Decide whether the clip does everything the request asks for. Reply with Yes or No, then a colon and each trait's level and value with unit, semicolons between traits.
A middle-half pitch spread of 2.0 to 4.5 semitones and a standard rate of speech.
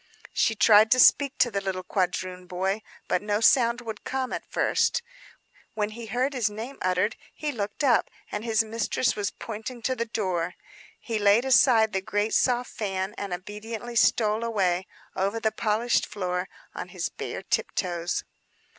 Yes: average, 3.4 semitones; average, 165 wpm